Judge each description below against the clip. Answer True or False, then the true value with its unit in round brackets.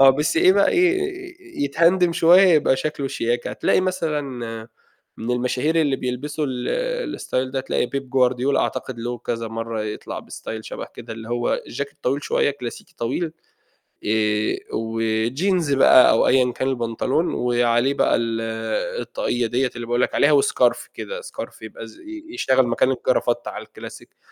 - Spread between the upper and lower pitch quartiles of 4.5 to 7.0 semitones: True (5.3 semitones)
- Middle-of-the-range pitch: False (130 Hz)